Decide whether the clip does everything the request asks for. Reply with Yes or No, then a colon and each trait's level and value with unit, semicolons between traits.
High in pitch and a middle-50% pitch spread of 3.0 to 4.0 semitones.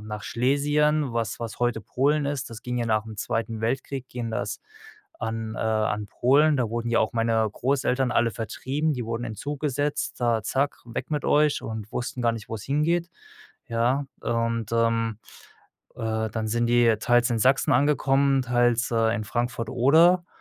No: low, 120 Hz; average, 3.4 semitones